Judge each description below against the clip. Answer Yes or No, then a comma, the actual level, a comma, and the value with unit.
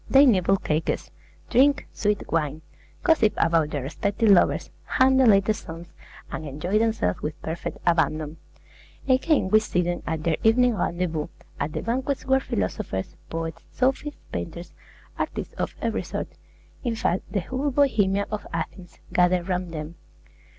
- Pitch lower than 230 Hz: Yes, medium, 185 Hz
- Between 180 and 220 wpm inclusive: No, average, 150 wpm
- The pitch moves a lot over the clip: Yes, wide, 6.1 semitones